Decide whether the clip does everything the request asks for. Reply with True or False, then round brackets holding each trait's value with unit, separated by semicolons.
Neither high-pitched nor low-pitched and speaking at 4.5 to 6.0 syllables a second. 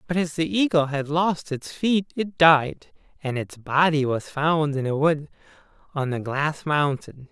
False (155 Hz; 4.1 syllables/s)